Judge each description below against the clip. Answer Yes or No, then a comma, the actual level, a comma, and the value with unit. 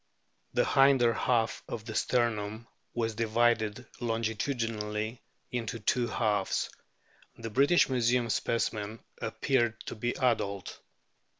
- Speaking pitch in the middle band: No, low, 115 Hz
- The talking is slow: Yes, slow, 105 wpm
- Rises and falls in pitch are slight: Yes, narrow, 1.9 semitones